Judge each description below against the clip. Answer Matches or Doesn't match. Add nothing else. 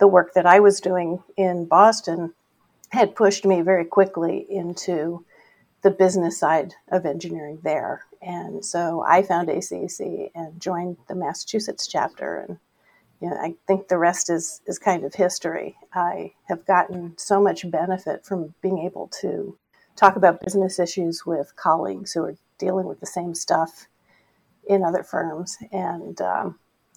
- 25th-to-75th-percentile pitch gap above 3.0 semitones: Doesn't match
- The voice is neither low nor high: Matches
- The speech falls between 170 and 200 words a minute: Doesn't match